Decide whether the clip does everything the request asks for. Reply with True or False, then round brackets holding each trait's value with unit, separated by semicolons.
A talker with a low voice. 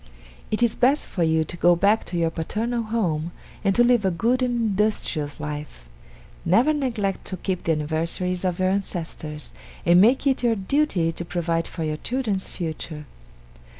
False (185 Hz)